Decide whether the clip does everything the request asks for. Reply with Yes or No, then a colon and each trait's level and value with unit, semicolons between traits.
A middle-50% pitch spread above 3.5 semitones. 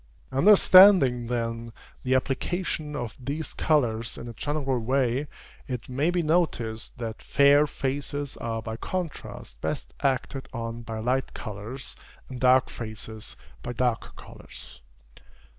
Yes: average, 3.9 semitones